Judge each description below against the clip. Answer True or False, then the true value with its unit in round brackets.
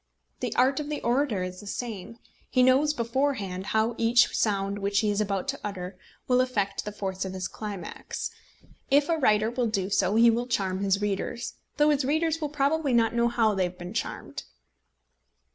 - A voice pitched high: True (220 Hz)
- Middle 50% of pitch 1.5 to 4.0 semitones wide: False (4.5 semitones)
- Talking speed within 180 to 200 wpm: True (195 wpm)